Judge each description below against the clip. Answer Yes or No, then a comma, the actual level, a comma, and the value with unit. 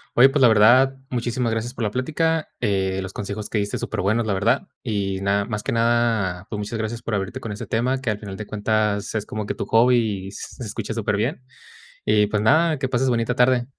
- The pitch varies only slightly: No, average, 3.1 semitones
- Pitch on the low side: Yes, low, 110 Hz